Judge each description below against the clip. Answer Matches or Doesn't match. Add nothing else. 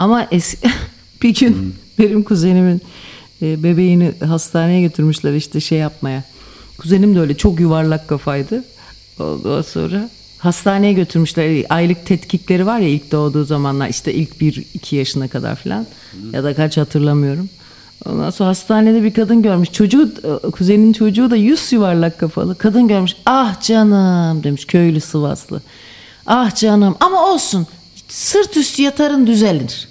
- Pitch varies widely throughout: Matches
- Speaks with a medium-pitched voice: Matches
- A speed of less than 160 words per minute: Matches